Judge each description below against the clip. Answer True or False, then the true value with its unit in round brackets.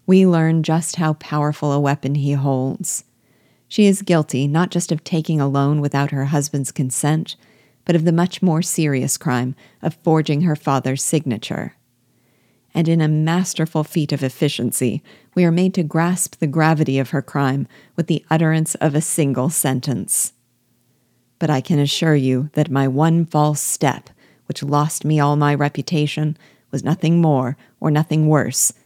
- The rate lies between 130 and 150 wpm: False (165 wpm)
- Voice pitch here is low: False (150 Hz)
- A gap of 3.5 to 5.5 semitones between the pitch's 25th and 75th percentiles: False (2.9 semitones)